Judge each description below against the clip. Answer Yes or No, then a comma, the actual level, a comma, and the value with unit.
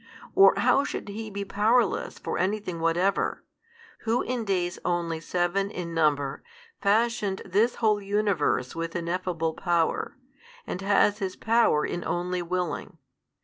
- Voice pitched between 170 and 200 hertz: Yes, medium, 185 Hz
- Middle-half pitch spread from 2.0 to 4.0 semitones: Yes, average, 3.5 semitones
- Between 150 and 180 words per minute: No, slow, 135 wpm